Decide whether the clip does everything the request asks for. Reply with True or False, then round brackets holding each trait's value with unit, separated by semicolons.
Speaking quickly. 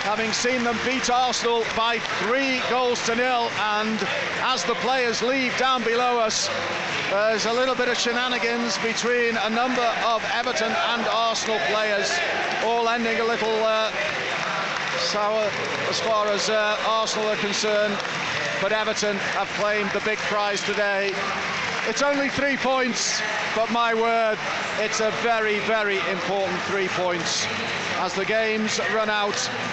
False (145 wpm)